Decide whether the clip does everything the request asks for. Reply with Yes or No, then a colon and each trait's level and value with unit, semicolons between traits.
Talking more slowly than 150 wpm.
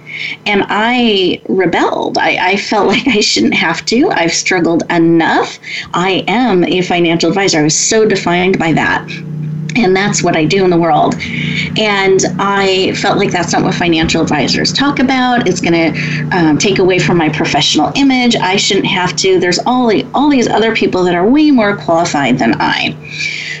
No: average, 185 wpm